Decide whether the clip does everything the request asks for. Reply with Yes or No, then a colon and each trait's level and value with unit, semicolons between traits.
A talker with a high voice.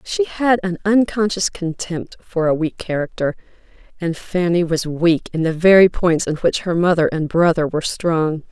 No: medium, 175 Hz